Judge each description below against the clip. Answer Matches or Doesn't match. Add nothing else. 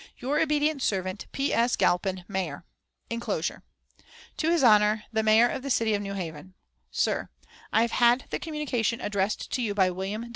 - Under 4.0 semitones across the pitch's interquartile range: Doesn't match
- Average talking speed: Matches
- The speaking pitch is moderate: Doesn't match